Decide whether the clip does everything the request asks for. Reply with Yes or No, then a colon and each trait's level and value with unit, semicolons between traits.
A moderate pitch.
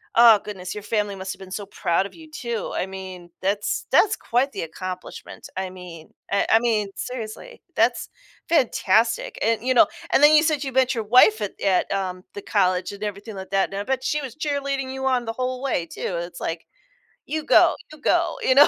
No: high, 215 Hz